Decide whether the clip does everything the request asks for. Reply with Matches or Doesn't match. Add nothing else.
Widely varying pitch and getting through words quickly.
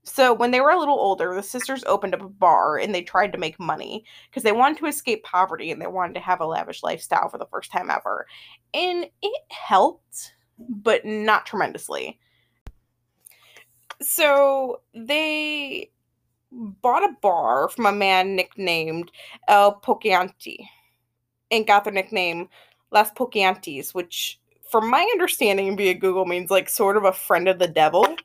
Doesn't match